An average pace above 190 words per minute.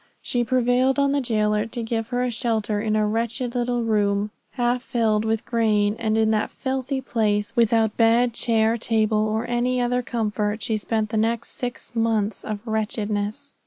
No: average, 175 wpm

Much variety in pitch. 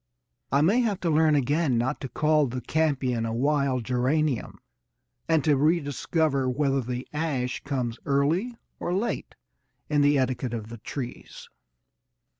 No: average, 3.5 semitones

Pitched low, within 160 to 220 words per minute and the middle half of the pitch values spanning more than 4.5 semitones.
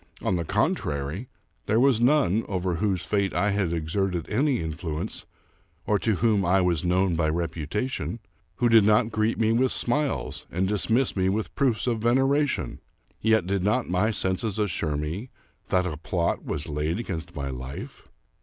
Yes: very low, 95 Hz; average, 170 wpm; average, 5.0 semitones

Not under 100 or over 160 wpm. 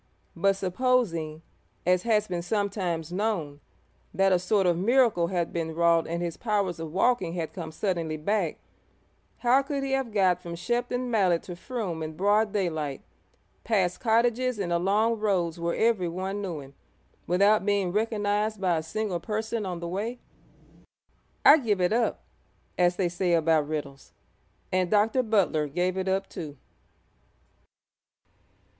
Yes: average, 150 wpm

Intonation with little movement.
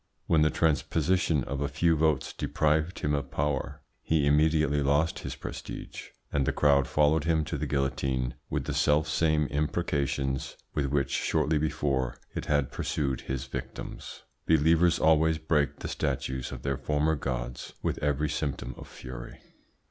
Yes: narrow, 2.3 semitones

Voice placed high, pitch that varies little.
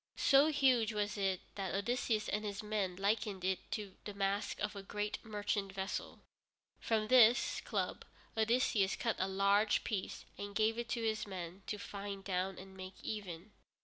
Yes: high, 205 Hz; narrow, 2.0 semitones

